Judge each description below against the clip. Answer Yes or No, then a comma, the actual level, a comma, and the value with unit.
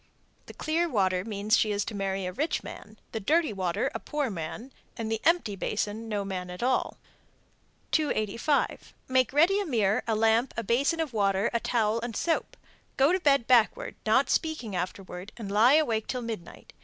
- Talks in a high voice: Yes, high, 225 Hz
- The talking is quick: No, average, 185 wpm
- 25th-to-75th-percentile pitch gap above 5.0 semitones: Yes, wide, 5.5 semitones